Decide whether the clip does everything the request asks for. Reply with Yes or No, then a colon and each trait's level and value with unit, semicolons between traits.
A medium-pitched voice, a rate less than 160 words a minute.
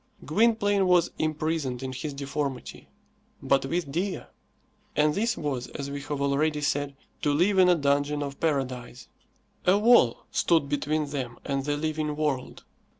Yes: medium, 145 Hz; average, 150 wpm